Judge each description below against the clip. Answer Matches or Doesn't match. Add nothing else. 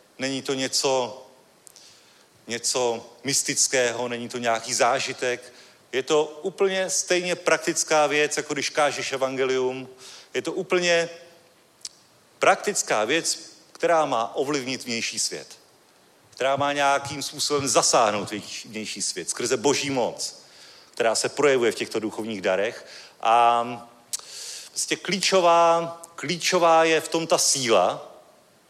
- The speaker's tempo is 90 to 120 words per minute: Matches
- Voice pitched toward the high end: Doesn't match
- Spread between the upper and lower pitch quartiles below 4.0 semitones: Doesn't match